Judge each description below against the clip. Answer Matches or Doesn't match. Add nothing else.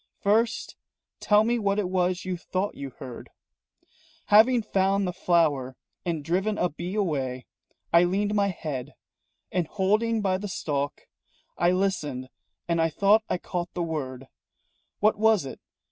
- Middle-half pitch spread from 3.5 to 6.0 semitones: Matches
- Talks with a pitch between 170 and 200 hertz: Matches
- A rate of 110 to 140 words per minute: Doesn't match